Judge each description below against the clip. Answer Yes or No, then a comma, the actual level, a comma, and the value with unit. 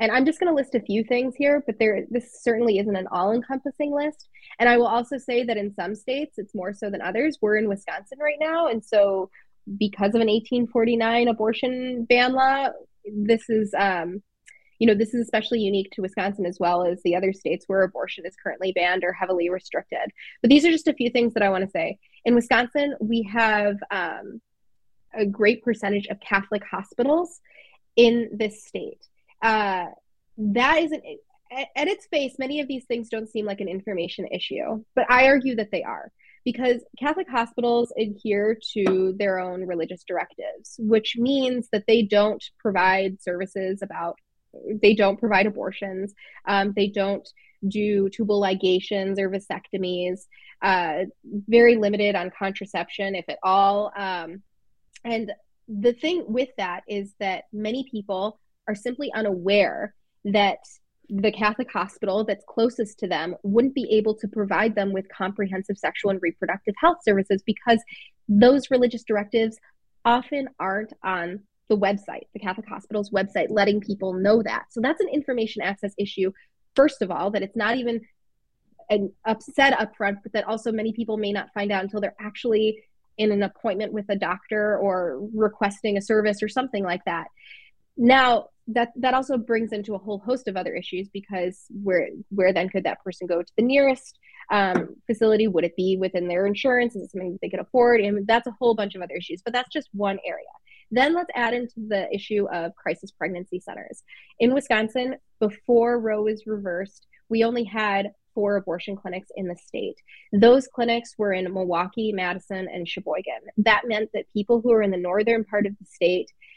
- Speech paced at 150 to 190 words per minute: Yes, average, 180 wpm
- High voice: Yes, high, 215 Hz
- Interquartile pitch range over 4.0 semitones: No, average, 3.4 semitones